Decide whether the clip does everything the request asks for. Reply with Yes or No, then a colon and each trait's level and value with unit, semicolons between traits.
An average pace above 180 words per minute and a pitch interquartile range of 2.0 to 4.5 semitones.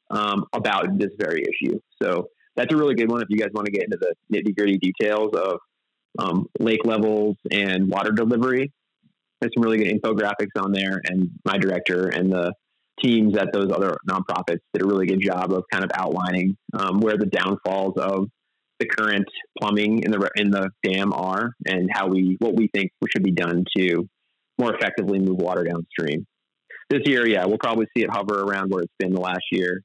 Yes: average, 200 wpm; average, 2.7 semitones